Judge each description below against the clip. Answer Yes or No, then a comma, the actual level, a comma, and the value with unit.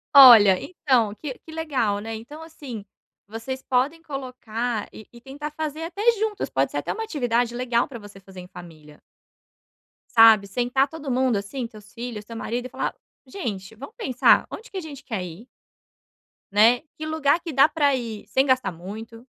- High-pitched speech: Yes, high, 245 Hz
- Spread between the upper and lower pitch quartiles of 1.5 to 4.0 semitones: No, average, 4.8 semitones